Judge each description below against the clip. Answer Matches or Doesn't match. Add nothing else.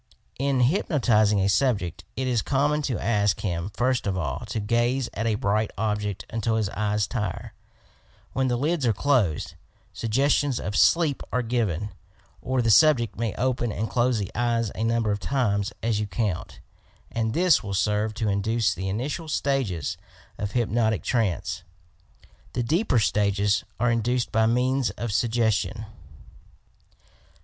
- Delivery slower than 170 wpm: Matches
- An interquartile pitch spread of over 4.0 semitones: Doesn't match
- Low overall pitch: Matches